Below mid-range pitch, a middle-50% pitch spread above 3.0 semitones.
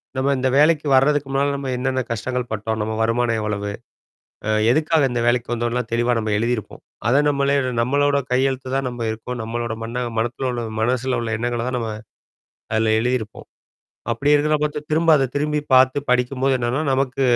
No: low, 125 Hz; average, 2.7 semitones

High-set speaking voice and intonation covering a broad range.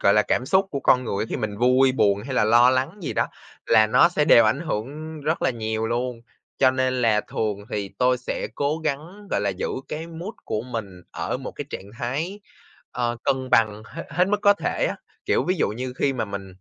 No: low, 125 Hz; wide, 5.8 semitones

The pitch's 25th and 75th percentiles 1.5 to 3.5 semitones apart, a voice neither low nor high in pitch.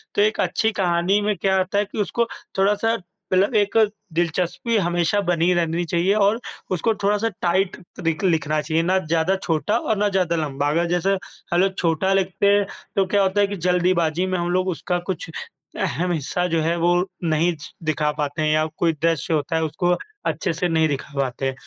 Yes: average, 3.1 semitones; medium, 175 Hz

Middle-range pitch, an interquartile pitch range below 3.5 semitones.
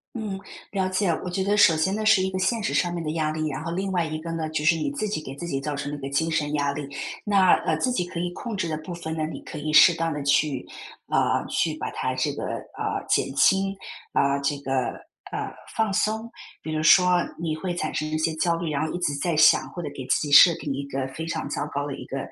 No: medium, 160 Hz; average, 3.9 semitones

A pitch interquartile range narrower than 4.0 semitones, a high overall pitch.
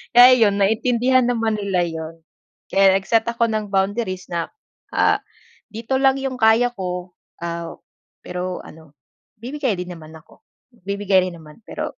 No: average, 4.7 semitones; high, 200 Hz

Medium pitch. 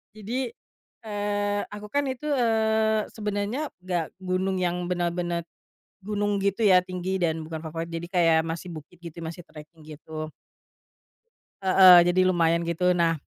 Yes: medium, 180 Hz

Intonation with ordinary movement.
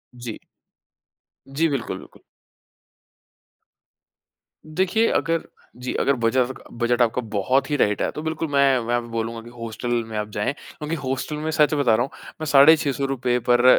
Yes: average, 4.0 semitones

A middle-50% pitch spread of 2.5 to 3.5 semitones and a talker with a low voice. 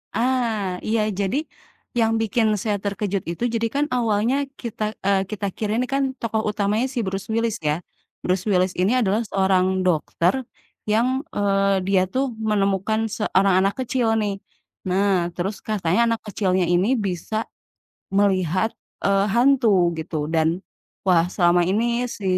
No: average, 3.0 semitones; high, 200 Hz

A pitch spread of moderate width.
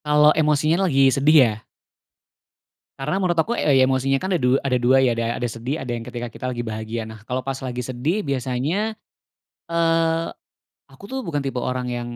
Yes: average, 4.2 semitones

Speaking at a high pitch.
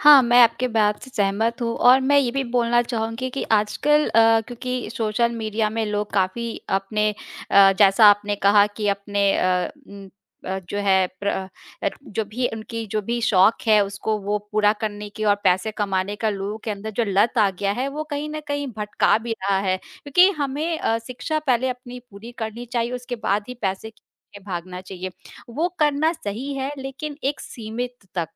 Yes: high, 220 Hz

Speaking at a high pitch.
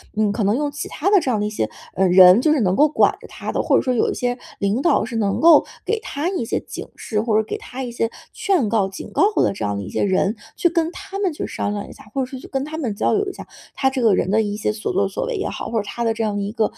Yes: high, 230 Hz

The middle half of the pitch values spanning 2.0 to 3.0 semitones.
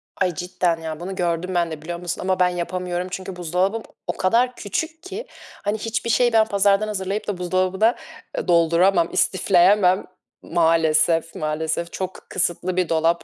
Yes: average, 2.7 semitones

